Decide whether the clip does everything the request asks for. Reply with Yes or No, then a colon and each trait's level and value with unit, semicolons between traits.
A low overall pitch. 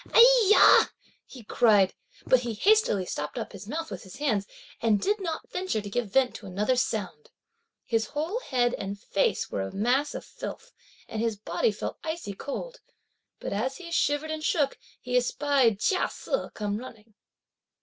No: high, 245 Hz